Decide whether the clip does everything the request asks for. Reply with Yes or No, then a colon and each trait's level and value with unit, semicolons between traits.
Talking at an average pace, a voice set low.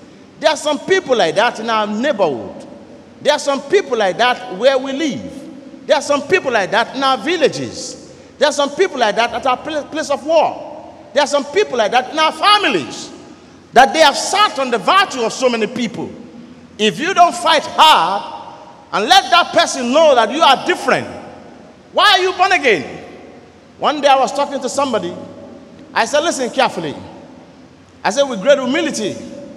No: average, 190 wpm; very high, 285 Hz